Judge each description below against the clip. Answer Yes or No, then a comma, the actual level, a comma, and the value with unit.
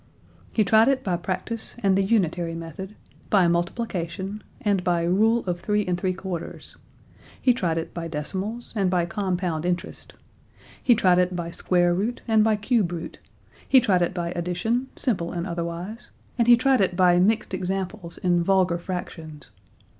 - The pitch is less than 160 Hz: No, medium, 185 Hz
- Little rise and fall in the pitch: No, average, 3.5 semitones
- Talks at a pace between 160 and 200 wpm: Yes, average, 170 wpm